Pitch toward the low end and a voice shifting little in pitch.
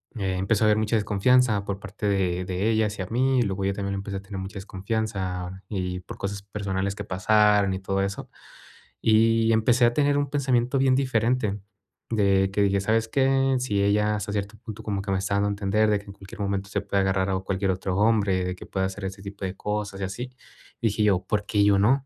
Yes: low, 100 Hz; narrow, 2.3 semitones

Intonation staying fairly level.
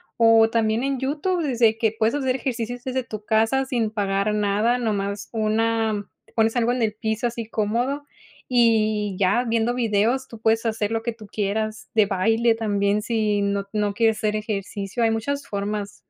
Yes: narrow, 2.0 semitones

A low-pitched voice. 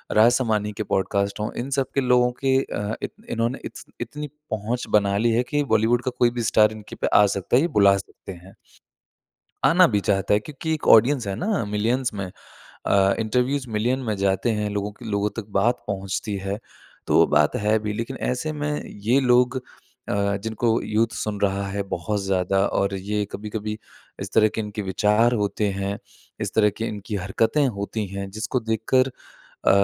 Yes: low, 110 Hz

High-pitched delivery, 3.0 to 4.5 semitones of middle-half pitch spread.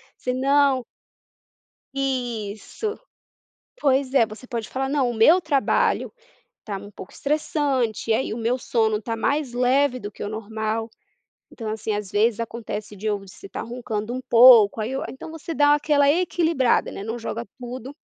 Yes: high, 245 Hz; average, 3.9 semitones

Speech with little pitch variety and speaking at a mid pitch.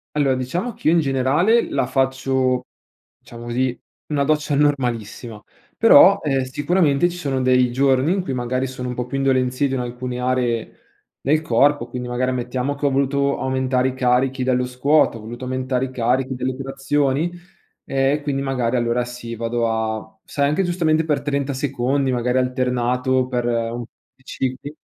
No: narrow, 2.2 semitones; low, 130 Hz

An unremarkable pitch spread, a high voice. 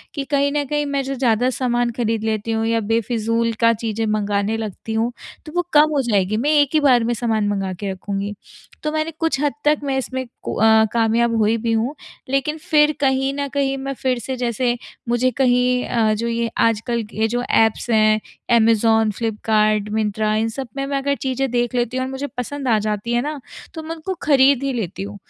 Yes: average, 3.6 semitones; high, 235 Hz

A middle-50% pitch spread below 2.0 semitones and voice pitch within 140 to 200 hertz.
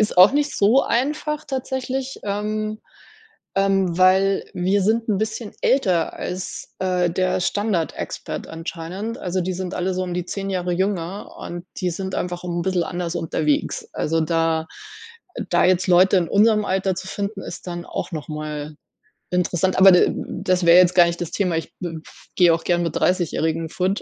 No: narrow, 2.6 semitones; medium, 185 Hz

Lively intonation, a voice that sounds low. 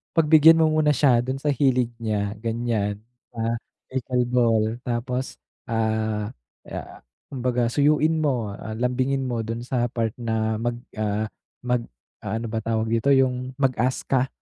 No: average, 2.7 semitones; low, 120 Hz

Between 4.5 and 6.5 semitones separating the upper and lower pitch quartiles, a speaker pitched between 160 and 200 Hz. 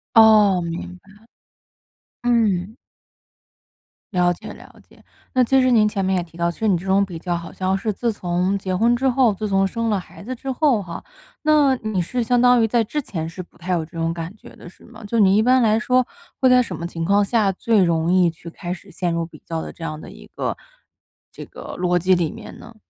Yes: average, 4.9 semitones; high, 195 Hz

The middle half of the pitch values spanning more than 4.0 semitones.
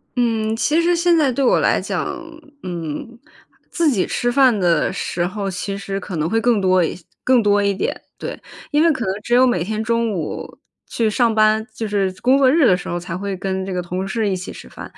Yes: average, 4.6 semitones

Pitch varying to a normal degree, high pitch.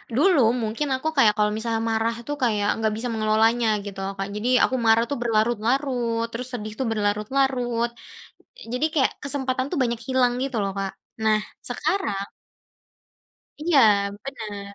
Yes: average, 3.3 semitones; high, 230 Hz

